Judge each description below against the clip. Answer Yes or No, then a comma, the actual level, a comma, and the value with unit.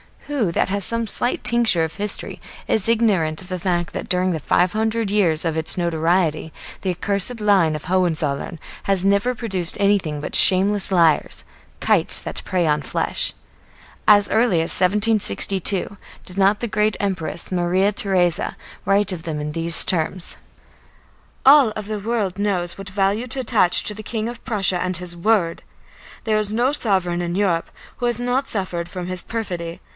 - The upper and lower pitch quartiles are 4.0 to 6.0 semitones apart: No, average, 3.6 semitones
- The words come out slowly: No, average, 170 wpm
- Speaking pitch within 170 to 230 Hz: Yes, high, 190 Hz